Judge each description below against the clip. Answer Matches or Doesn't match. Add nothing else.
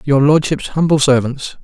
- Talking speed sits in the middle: Matches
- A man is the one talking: Matches